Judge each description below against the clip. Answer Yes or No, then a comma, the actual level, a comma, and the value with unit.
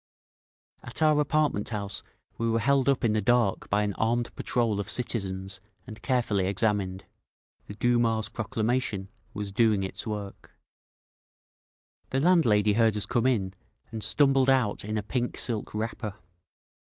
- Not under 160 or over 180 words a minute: No, average, 145 wpm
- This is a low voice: Yes, low, 110 Hz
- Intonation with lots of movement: No, average, 3.1 semitones